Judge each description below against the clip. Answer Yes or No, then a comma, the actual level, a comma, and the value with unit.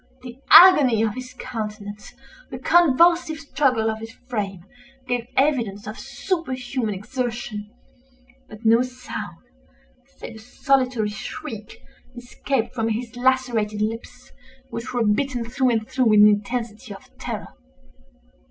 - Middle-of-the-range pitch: No, high, 235 Hz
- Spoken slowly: Yes, slow, 125 wpm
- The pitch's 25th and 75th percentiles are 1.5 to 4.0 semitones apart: Yes, average, 3.1 semitones